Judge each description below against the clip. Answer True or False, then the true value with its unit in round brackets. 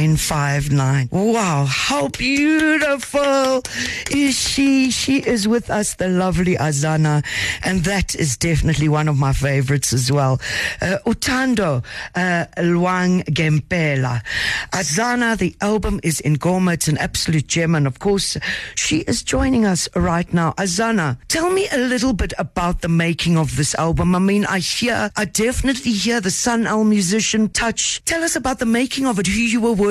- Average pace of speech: True (165 wpm)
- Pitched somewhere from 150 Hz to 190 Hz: True (185 Hz)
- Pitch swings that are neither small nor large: False (6.9 semitones)